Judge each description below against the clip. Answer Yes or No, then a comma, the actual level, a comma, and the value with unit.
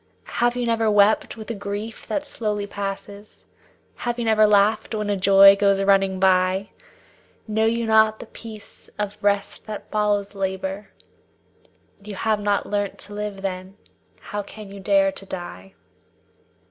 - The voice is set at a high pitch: Yes, high, 205 Hz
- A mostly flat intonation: Yes, narrow, 1.7 semitones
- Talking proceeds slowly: No, average, 155 wpm